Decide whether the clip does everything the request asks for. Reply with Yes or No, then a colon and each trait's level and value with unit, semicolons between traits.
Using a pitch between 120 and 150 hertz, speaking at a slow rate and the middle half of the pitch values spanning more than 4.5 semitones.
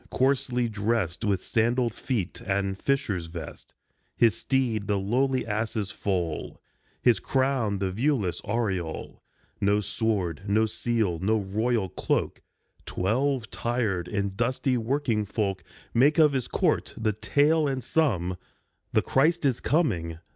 No: low, 110 Hz; slow, 130 wpm; average, 4.9 semitones